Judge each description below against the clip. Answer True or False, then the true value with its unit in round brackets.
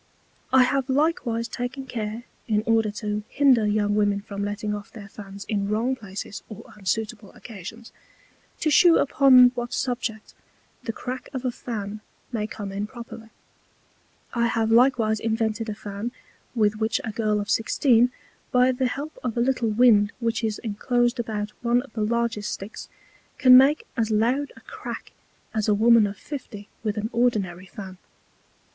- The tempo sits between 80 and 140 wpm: False (165 wpm)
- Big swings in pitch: False (2.9 semitones)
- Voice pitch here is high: True (225 Hz)